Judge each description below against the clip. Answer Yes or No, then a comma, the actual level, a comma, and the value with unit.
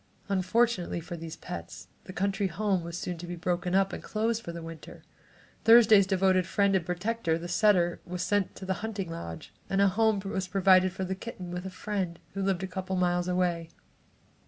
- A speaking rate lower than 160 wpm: No, fast, 205 wpm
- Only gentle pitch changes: Yes, narrow, 2.1 semitones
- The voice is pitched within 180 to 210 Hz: Yes, medium, 185 Hz